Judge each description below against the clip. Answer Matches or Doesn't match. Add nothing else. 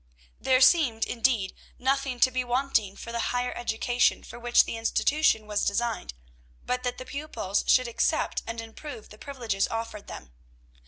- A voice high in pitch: Matches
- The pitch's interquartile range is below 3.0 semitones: Matches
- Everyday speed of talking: Matches